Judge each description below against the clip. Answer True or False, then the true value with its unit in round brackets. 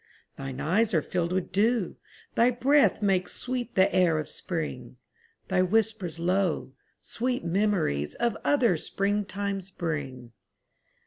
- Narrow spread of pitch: False (4.9 semitones)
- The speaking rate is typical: False (125 wpm)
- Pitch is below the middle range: False (190 Hz)